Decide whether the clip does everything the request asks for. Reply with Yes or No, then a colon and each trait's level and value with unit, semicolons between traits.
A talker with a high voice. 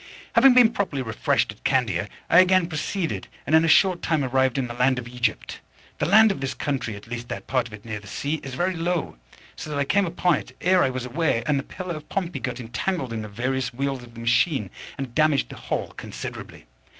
No: low, 135 Hz